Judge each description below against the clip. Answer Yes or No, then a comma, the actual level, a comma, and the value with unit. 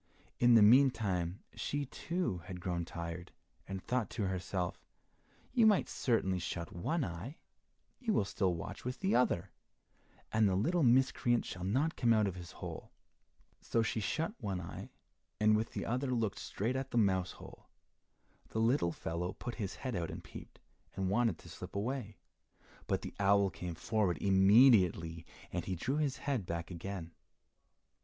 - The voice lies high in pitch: No, low, 100 Hz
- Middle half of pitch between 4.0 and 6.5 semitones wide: Yes, wide, 5.6 semitones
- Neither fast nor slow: Yes, average, 165 wpm